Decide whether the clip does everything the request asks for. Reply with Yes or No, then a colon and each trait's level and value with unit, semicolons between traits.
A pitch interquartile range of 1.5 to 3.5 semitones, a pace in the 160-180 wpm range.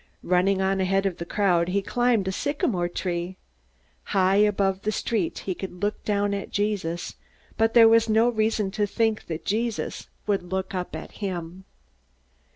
Yes: narrow, 2.6 semitones; average, 165 wpm